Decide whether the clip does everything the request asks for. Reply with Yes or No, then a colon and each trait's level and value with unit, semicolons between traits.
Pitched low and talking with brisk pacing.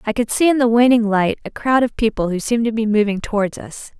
No: high, 225 Hz; fast, 270 wpm